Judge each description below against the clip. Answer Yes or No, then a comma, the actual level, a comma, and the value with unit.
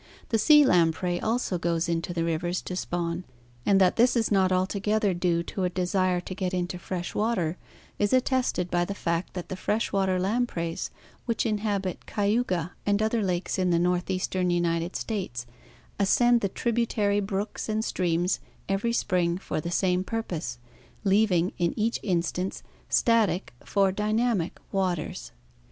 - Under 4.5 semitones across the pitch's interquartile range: Yes, average, 3.2 semitones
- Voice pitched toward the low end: No, medium, 185 Hz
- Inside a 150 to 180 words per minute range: Yes, average, 155 wpm